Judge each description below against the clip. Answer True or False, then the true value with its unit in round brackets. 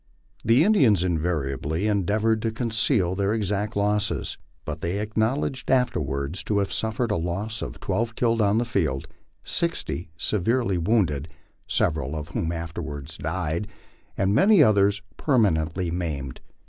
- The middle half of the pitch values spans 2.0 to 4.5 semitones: False (5.2 semitones)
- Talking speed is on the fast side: False (135 wpm)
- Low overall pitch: True (100 Hz)